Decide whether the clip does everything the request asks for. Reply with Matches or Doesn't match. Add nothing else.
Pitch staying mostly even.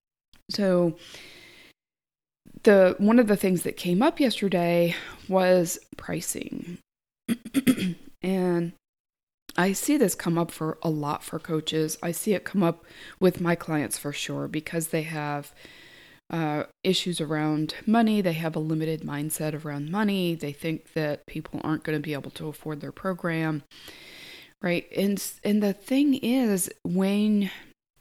Doesn't match